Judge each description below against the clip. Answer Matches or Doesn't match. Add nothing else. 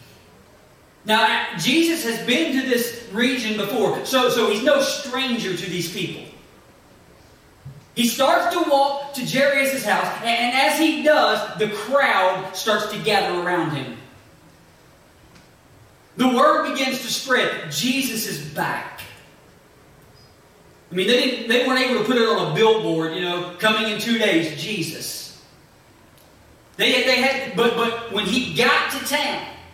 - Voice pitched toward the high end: Matches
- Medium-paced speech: Matches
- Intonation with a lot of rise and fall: Doesn't match